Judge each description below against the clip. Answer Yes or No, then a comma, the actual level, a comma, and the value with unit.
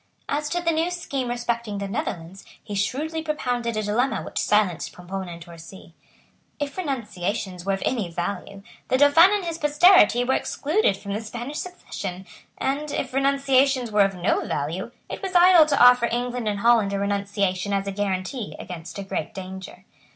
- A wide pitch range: Yes, wide, 6.3 semitones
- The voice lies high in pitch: Yes, high, 220 Hz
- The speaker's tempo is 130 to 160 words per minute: No, average, 175 wpm